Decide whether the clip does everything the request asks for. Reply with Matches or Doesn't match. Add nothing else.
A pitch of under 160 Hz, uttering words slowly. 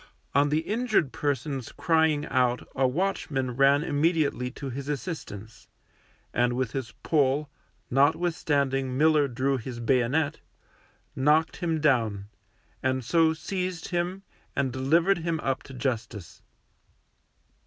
Matches